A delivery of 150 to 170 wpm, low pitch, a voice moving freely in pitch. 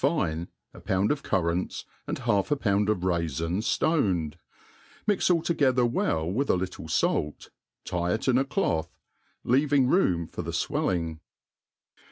Yes: average, 160 wpm; very low, 95 Hz; wide, 8.2 semitones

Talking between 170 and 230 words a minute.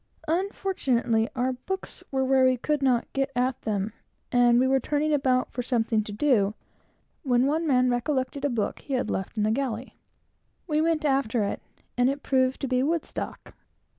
Yes: average, 180 wpm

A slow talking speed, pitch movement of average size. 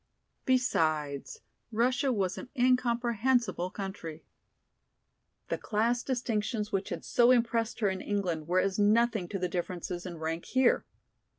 Yes: slow, 130 wpm; average, 5.0 semitones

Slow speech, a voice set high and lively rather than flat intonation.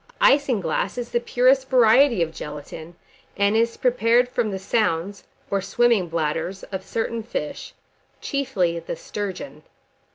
Yes: slow, 130 wpm; high, 215 Hz; wide, 5.8 semitones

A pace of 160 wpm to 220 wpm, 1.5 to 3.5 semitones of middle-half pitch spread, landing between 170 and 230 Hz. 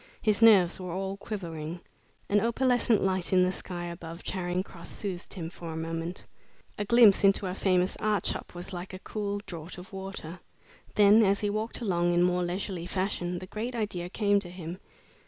Yes: average, 190 wpm; narrow, 2.6 semitones; medium, 185 Hz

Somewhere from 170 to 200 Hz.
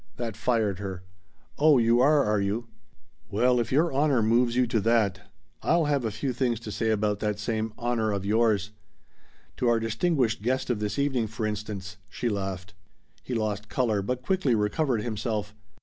No: low, 115 Hz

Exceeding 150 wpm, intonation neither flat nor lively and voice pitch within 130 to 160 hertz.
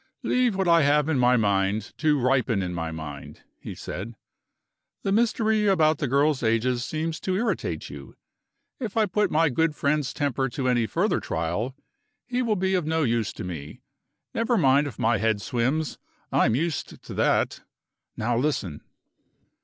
No: average, 170 wpm; wide, 6.8 semitones; medium, 140 Hz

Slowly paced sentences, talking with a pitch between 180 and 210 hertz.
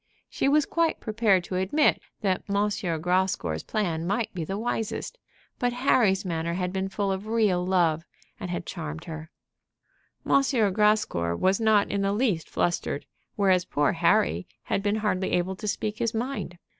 No: average, 165 wpm; high, 190 Hz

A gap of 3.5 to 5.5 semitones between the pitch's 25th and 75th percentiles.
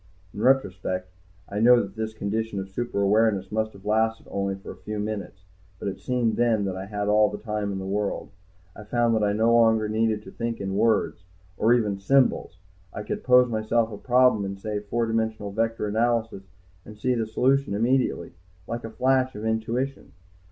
No: narrow, 2.5 semitones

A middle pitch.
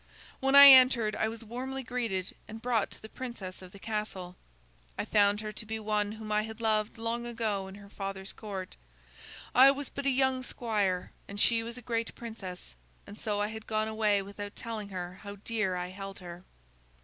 No: high, 215 Hz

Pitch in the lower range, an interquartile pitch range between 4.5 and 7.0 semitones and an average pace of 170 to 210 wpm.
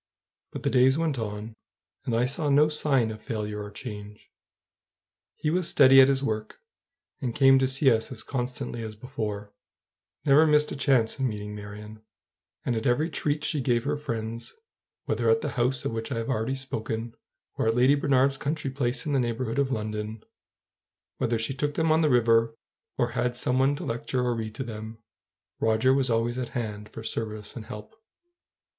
No: low, 120 Hz; average, 3.5 semitones; average, 190 wpm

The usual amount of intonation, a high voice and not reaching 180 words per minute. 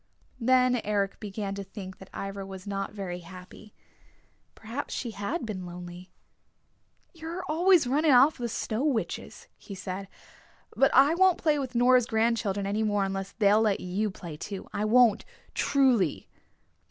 Yes: average, 4.5 semitones; high, 215 Hz; average, 155 wpm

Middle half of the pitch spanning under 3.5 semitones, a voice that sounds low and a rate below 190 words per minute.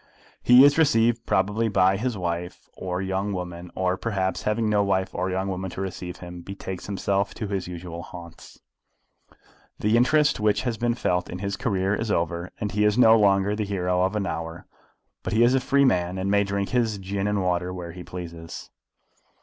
No: average, 2.8 semitones; very low, 95 Hz; average, 200 wpm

